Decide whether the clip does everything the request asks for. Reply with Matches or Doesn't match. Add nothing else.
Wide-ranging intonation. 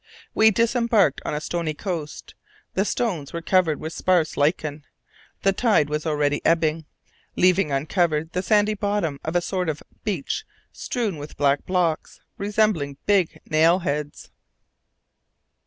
Doesn't match